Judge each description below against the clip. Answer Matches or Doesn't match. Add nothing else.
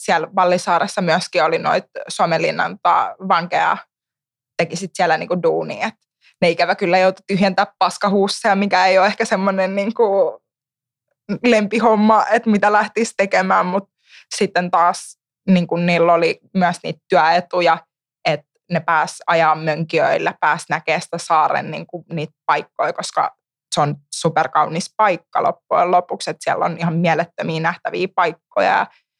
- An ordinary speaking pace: Matches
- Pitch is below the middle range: Doesn't match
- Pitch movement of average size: Matches